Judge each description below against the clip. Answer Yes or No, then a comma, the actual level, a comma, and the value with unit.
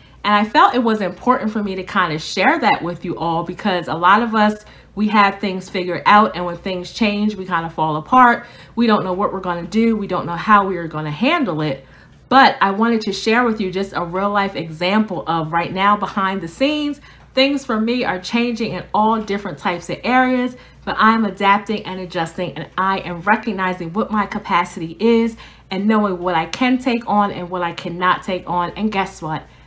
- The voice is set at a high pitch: Yes, high, 195 Hz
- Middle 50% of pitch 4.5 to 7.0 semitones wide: No, average, 3.8 semitones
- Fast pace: Yes, fast, 225 wpm